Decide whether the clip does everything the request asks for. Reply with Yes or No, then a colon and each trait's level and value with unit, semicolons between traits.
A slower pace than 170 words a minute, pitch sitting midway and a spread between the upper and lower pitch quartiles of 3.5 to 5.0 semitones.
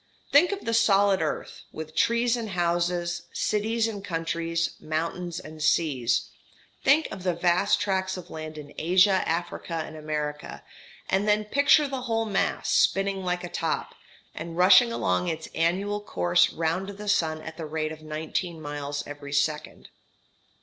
Yes: average, 155 wpm; medium, 175 Hz; average, 4.3 semitones